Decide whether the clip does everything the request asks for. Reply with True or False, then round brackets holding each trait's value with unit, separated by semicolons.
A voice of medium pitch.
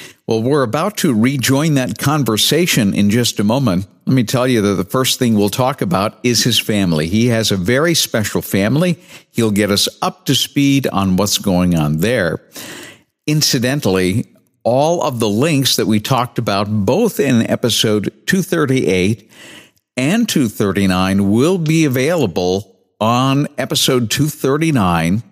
False (120 Hz)